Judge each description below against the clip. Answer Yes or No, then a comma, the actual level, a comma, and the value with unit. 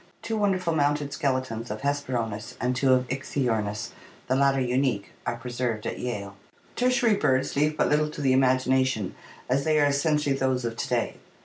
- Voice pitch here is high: No, low, 130 Hz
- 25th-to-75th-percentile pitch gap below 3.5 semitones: Yes, average, 2.8 semitones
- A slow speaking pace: No, average, 175 wpm